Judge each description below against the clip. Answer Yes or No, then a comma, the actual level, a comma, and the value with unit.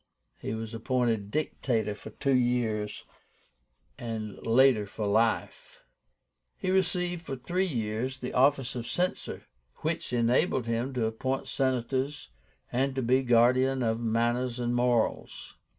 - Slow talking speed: Yes, slow, 130 wpm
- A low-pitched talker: Yes, low, 125 Hz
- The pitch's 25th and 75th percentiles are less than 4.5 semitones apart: Yes, average, 2.8 semitones